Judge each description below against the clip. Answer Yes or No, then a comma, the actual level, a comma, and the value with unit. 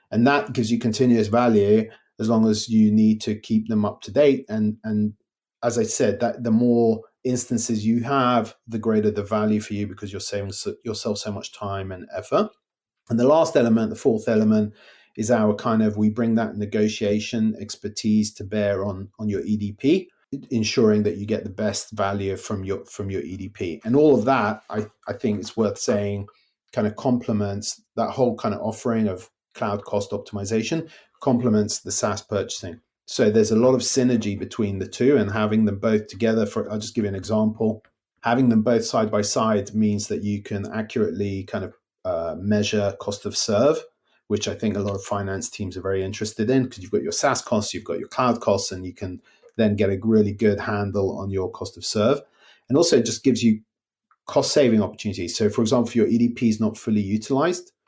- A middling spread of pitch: No, narrow, 1.9 semitones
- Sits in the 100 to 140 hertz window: Yes, low, 110 Hz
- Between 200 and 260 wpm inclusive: Yes, fast, 205 wpm